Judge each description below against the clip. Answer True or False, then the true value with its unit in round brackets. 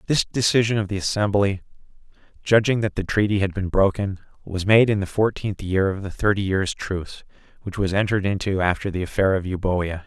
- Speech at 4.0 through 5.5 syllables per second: False (5.7 syllables/s)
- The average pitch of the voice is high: False (100 Hz)